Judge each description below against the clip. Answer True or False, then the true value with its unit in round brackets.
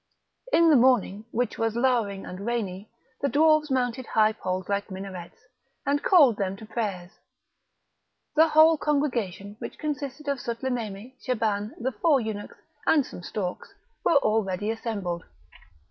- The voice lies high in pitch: True (225 Hz)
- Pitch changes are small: False (5.2 semitones)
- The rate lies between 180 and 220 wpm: False (140 wpm)